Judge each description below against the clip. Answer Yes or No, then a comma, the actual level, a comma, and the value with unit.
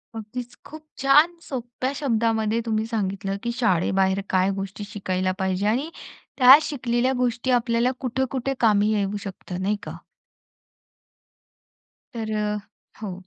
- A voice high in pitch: Yes, high, 225 Hz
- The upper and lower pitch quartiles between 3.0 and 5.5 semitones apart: Yes, average, 4.2 semitones